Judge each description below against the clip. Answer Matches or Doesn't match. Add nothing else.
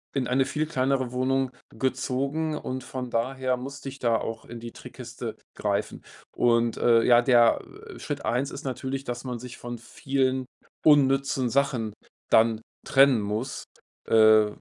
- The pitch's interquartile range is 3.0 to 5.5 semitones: Doesn't match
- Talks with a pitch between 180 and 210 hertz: Doesn't match